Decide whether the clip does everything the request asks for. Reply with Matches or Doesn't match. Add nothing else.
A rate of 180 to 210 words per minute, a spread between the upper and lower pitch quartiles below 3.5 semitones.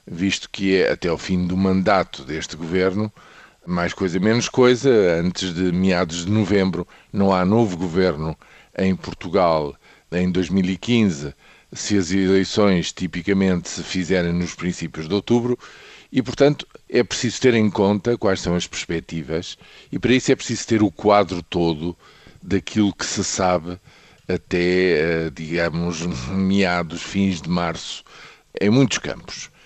Doesn't match